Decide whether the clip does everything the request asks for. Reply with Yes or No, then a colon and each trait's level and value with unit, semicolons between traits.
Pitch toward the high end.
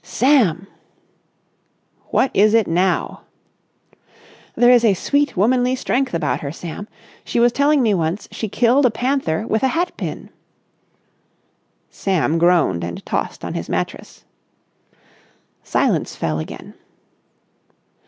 Yes: high, 215 Hz